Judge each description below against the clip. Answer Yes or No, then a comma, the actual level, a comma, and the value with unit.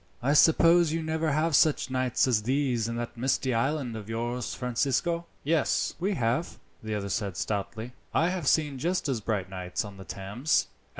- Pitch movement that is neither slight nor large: No, wide, 5.9 semitones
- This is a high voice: No, low, 130 Hz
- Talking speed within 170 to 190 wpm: Yes, average, 180 wpm